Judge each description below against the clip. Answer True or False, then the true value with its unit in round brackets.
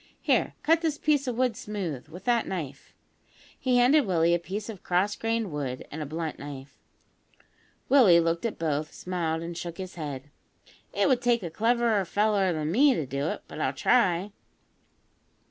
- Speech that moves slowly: False (180 wpm)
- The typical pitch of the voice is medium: True (180 Hz)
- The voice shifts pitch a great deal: True (6.6 semitones)